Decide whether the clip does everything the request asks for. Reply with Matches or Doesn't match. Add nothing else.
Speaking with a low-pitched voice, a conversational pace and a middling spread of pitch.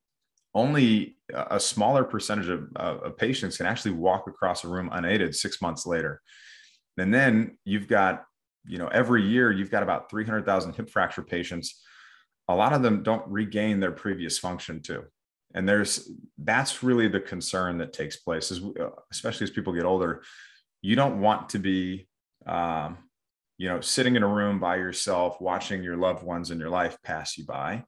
Matches